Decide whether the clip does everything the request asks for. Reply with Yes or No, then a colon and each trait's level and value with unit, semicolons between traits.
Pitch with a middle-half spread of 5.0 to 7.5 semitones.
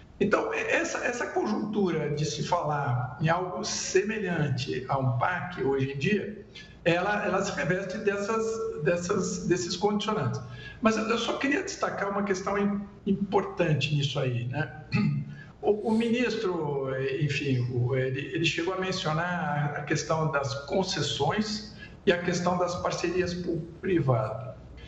Yes: wide, 5.6 semitones